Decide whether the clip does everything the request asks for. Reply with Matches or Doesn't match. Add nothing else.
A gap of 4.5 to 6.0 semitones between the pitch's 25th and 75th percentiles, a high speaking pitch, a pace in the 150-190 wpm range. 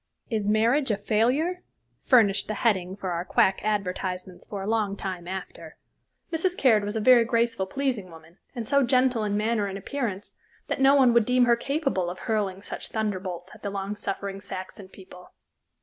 Doesn't match